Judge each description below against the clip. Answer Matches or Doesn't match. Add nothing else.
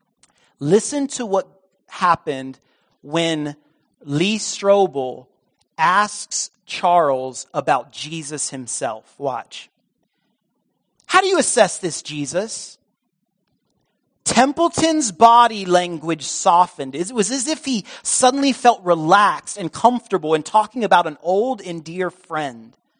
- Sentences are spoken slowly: Matches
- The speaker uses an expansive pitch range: Matches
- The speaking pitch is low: Doesn't match